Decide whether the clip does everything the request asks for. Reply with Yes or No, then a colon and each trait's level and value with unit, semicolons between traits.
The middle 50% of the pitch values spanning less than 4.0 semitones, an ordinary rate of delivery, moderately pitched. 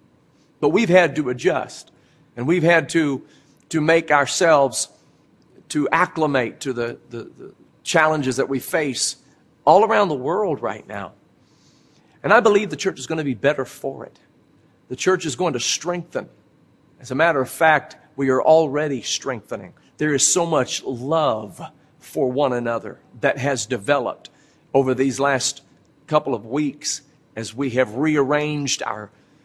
Yes: average, 3.0 semitones; average, 155 wpm; medium, 145 Hz